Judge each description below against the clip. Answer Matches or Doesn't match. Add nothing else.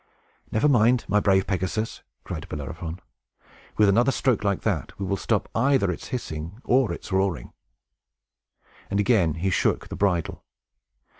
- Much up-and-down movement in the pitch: Doesn't match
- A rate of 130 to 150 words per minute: Matches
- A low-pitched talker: Matches